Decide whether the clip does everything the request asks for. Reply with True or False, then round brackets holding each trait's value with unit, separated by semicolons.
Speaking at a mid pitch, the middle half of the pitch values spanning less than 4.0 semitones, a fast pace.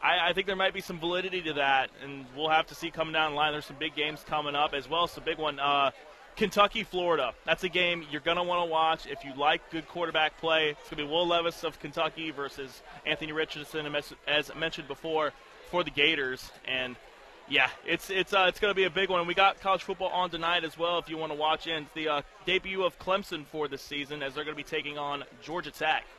True (160 Hz; 2.8 semitones; 245 wpm)